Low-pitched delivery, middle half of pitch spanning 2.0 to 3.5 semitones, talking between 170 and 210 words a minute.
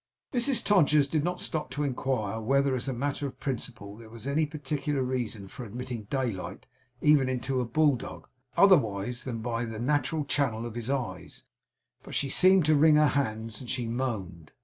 No: low, 130 Hz; average, 4.2 semitones; average, 180 wpm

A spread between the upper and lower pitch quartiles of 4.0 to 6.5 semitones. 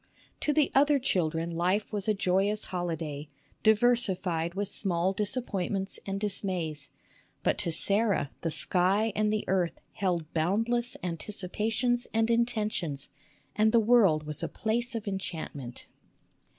Yes: average, 4.5 semitones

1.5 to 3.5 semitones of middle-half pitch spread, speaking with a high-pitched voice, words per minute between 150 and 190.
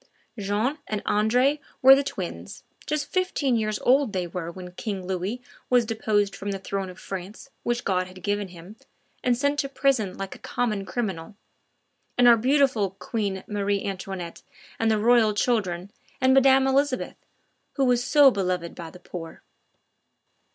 No: average, 4.8 semitones; high, 215 Hz; average, 160 wpm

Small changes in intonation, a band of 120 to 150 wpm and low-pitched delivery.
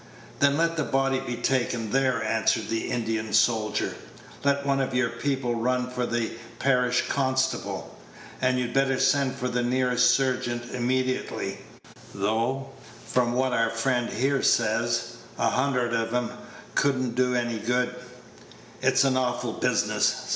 Yes: narrow, 1.8 semitones; average, 145 wpm; low, 125 Hz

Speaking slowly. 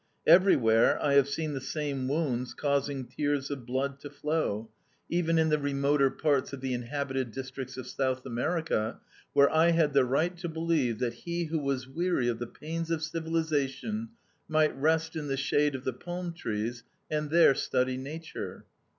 No: average, 175 wpm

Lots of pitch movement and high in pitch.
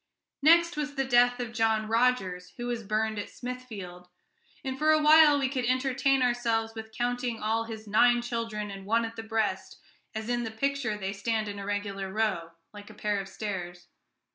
No: average, 3.2 semitones; high, 225 Hz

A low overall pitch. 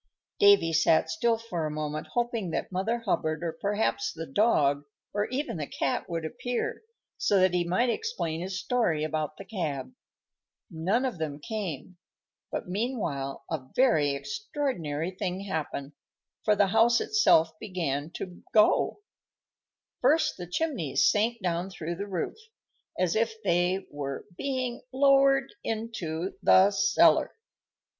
No: medium, 185 Hz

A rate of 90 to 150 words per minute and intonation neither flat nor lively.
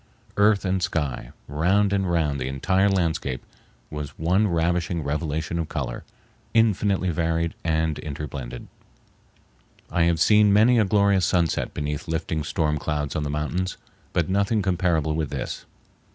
Yes: average, 140 wpm; average, 4.1 semitones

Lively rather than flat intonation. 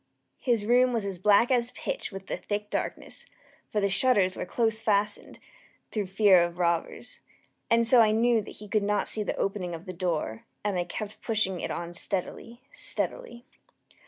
No: average, 3.7 semitones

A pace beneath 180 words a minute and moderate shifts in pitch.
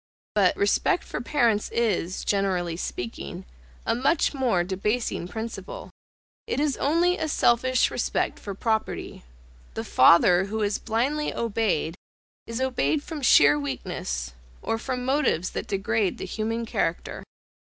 No: slow, 135 wpm; wide, 6.1 semitones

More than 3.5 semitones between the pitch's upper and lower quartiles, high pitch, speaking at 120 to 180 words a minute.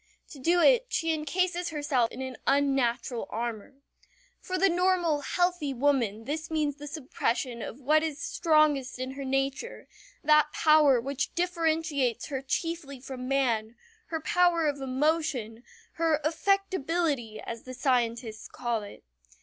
Yes: average, 4.2 semitones; very high, 285 Hz; average, 140 wpm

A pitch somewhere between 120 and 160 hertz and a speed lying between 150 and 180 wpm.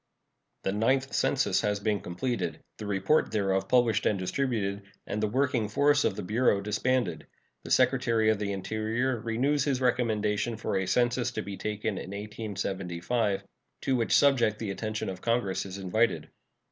No: low, 110 Hz; average, 160 wpm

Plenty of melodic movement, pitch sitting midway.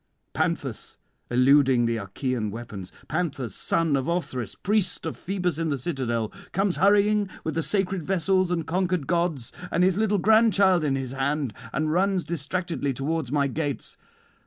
Yes: wide, 5.7 semitones; medium, 160 Hz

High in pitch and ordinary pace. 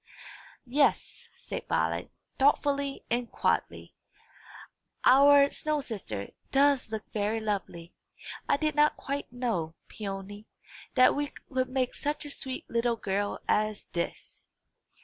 No: very high, 250 Hz; slow, 120 wpm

